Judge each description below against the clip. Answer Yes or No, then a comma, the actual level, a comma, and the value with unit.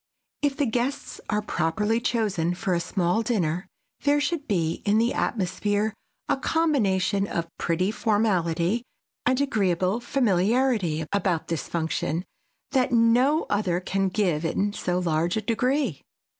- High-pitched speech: Yes, high, 205 Hz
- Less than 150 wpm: Yes, slow, 135 wpm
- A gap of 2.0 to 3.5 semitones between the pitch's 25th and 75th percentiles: No, average, 5.3 semitones